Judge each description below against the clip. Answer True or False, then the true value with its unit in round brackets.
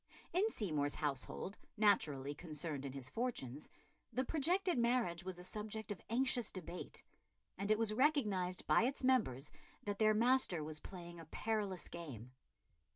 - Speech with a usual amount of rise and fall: False (7.4 semitones)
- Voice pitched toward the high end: True (195 Hz)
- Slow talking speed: False (150 wpm)